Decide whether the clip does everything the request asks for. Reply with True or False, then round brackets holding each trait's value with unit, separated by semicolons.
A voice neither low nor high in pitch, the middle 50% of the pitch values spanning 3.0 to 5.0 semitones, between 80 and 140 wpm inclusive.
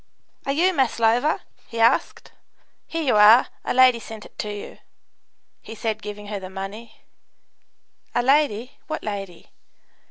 False (225 Hz; 3.7 semitones; 135 wpm)